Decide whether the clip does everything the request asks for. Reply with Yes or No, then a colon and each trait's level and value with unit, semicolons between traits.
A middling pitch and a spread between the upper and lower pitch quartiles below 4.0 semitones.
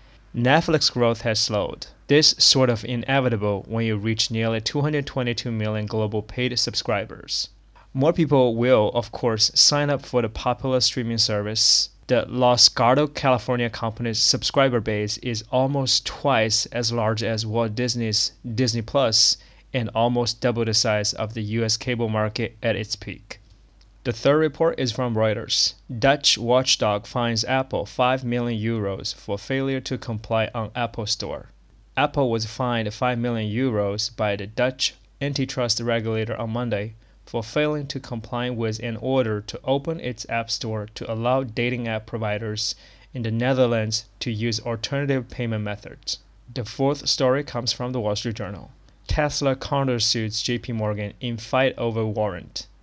No: low, 120 Hz; average, 2.9 semitones